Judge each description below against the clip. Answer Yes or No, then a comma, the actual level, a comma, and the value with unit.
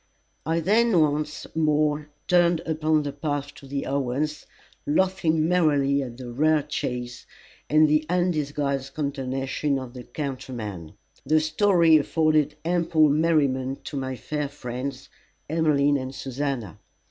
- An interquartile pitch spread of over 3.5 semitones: No, narrow, 2.6 semitones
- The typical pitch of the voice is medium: Yes, medium, 145 Hz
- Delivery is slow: Yes, slow, 125 wpm